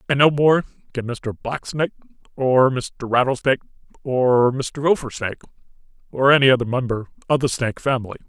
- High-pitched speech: No, low, 130 Hz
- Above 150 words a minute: No, average, 145 wpm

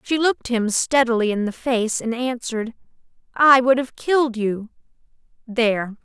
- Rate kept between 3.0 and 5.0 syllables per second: Yes, 4.8 syllables/s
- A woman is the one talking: Yes, female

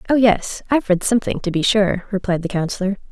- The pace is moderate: No, fast, 210 wpm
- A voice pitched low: No, high, 200 Hz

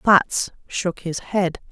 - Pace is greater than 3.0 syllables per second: No, 2.9 syllables/s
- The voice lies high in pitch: No, medium, 180 Hz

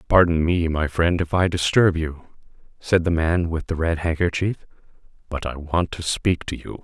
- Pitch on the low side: Yes, very low, 85 Hz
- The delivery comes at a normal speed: Yes, average, 195 wpm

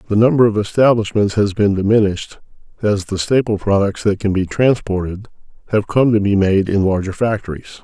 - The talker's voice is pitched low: Yes, low, 105 Hz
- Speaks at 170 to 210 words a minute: Yes, average, 175 wpm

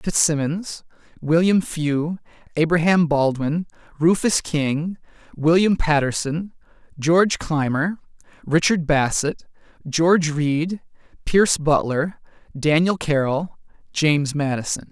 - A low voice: No, medium, 160 Hz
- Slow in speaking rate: Yes, slow, 85 wpm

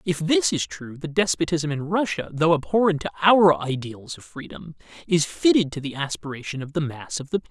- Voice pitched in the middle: Yes, medium, 160 Hz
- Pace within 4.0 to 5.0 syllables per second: No, 5.5 syllables/s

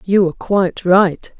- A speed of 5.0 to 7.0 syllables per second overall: No, 4.7 syllables/s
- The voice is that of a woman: Yes, female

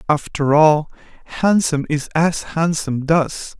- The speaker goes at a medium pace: No, slow, 115 wpm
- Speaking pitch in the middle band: Yes, medium, 155 Hz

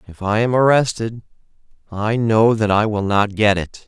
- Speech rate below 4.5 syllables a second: No, 4.6 syllables/s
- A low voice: Yes, low, 110 Hz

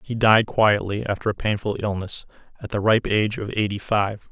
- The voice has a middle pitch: No, low, 105 Hz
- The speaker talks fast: No, average, 195 wpm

